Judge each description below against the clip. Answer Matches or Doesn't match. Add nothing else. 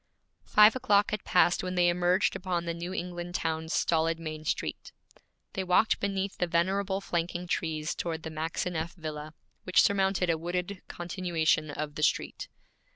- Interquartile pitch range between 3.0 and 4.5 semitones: Doesn't match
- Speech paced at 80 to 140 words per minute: Doesn't match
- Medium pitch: Matches